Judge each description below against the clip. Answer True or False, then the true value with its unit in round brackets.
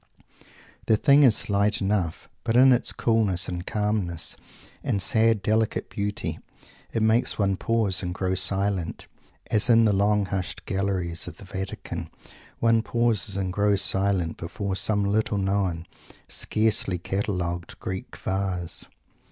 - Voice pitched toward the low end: True (100 Hz)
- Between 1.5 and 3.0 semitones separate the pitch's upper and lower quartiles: True (2.7 semitones)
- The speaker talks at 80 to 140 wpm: True (135 wpm)